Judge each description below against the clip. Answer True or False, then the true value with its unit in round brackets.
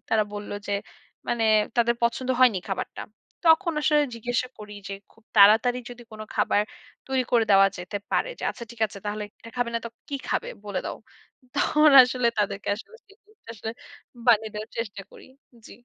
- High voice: True (230 Hz)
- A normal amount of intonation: True (3.3 semitones)